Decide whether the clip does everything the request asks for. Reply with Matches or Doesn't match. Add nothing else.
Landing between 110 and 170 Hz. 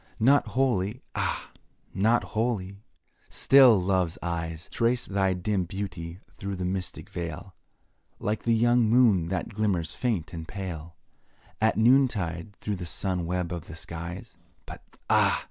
Doesn't match